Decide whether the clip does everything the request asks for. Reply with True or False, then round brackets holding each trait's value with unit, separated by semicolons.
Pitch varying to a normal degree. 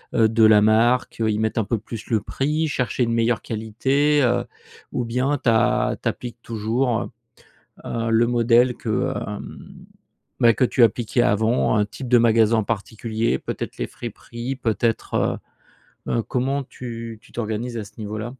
False (1.8 semitones)